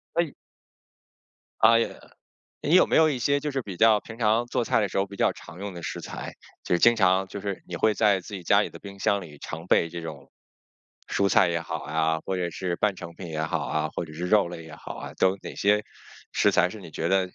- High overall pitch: No, very low, 95 Hz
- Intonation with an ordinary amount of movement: Yes, average, 4.0 semitones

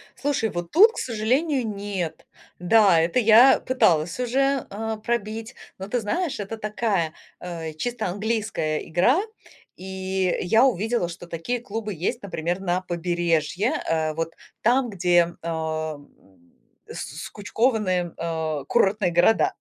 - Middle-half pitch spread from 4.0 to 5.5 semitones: Yes, average, 5.1 semitones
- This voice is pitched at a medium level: No, high, 200 Hz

